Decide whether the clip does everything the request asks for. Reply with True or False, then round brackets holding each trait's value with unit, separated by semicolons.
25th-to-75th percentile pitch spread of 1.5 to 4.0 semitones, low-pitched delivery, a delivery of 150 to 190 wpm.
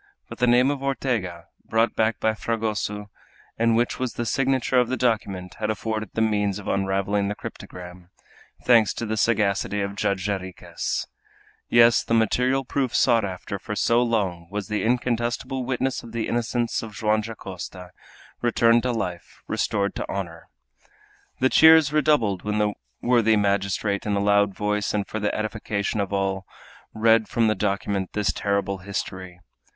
True (2.9 semitones; 105 Hz; 165 wpm)